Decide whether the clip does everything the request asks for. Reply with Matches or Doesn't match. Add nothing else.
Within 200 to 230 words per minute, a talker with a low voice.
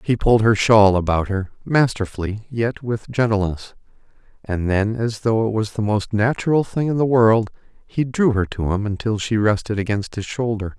Doesn't match